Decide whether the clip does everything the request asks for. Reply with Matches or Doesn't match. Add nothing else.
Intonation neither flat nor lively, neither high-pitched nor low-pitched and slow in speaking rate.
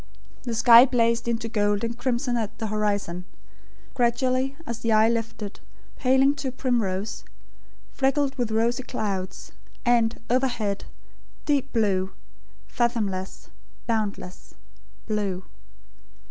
Doesn't match